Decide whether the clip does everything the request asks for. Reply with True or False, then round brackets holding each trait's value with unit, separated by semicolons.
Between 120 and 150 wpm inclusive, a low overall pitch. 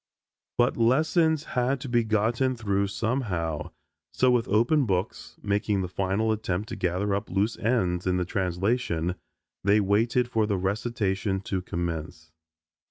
True (145 wpm; 105 Hz)